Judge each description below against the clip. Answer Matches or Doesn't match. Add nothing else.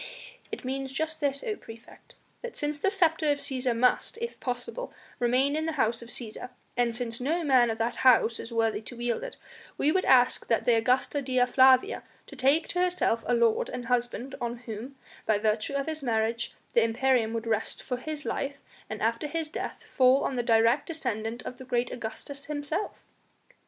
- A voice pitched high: Matches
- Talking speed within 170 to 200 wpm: Matches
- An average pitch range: Matches